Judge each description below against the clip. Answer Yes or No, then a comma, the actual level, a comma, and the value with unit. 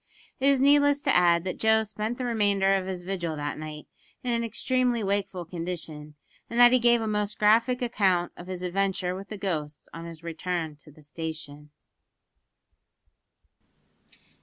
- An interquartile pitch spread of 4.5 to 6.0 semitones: Yes, average, 5.2 semitones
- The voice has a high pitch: Yes, high, 195 Hz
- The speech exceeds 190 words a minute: No, average, 165 wpm